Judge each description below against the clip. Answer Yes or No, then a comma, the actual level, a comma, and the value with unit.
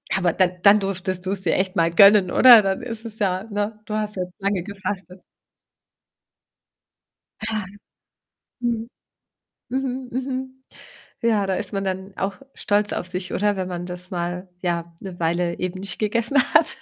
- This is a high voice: Yes, high, 195 Hz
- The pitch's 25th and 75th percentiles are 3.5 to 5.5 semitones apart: No, average, 2.9 semitones